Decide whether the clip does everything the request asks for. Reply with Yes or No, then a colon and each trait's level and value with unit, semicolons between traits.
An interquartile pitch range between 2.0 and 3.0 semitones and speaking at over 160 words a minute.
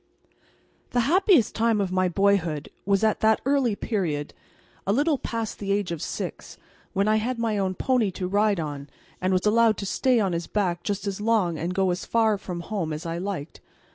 No: average, 3.8 semitones; average, 200 wpm